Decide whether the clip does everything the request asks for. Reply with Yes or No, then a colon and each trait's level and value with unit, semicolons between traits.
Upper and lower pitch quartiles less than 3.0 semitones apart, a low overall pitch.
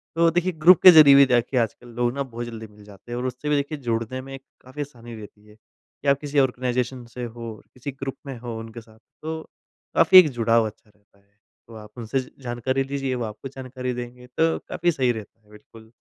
No: average, 3.4 semitones; low, 125 Hz